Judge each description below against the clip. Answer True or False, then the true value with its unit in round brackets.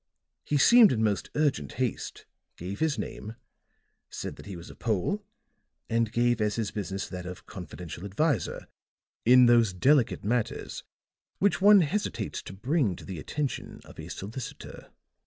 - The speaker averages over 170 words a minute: False (155 wpm)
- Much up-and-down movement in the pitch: True (6.6 semitones)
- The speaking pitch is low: True (115 Hz)